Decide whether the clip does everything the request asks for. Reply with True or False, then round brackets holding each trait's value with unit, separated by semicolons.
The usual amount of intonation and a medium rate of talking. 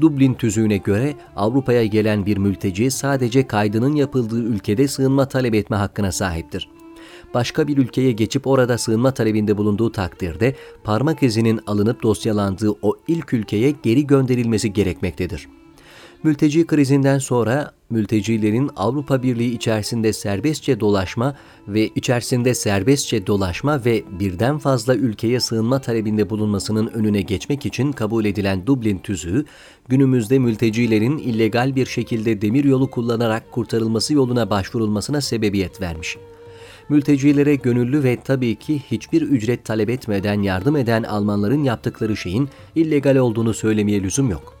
True (4.2 semitones; 125 wpm)